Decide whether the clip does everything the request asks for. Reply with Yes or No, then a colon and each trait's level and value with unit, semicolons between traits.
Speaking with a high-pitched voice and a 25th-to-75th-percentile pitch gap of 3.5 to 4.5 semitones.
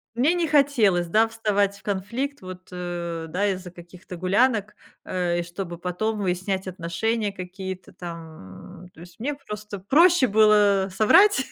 Yes: high, 195 Hz; average, 3.8 semitones